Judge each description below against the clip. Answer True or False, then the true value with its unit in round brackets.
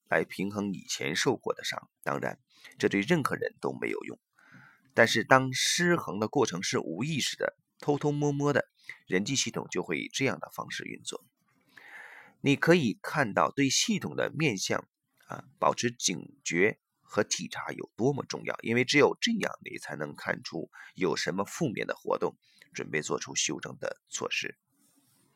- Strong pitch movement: True (6.8 semitones)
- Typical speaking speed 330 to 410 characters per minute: False (245 characters per minute)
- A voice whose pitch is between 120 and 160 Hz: True (140 Hz)